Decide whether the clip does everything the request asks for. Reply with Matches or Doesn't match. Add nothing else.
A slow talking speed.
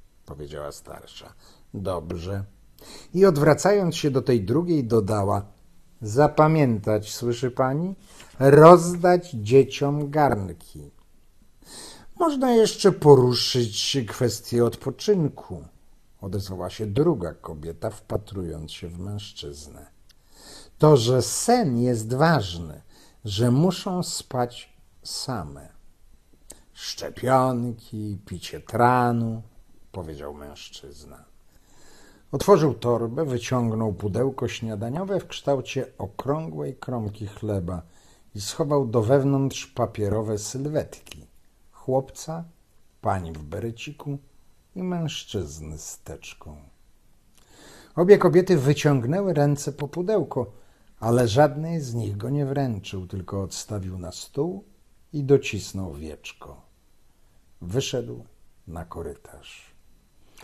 Matches